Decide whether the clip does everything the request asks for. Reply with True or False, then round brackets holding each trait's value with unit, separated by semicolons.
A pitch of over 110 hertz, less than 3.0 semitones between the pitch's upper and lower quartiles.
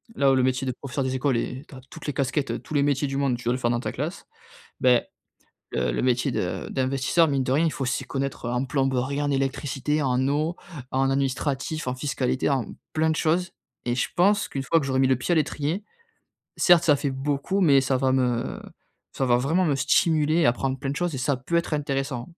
True (135 Hz; 2.4 semitones)